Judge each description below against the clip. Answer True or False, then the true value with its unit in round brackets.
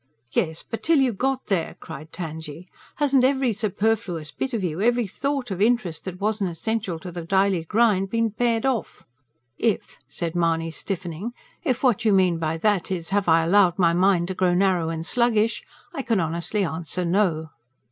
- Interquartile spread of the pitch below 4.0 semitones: False (5.2 semitones)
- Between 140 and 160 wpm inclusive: False (180 wpm)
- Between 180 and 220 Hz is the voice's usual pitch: True (190 Hz)